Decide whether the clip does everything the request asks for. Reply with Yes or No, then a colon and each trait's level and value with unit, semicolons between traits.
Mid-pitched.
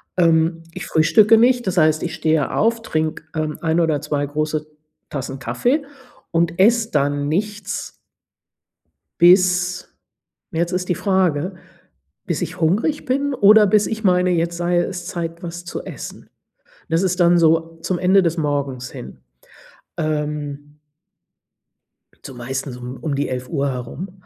Yes: medium, 170 Hz